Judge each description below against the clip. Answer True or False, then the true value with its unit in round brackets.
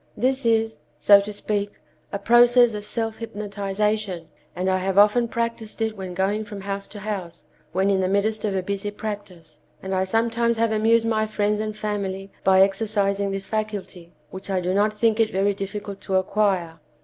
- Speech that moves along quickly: False (185 wpm)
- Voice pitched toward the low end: False (205 Hz)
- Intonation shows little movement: True (2.1 semitones)